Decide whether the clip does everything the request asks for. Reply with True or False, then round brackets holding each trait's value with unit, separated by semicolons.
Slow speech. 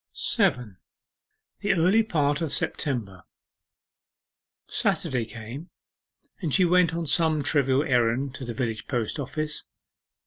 True (115 wpm)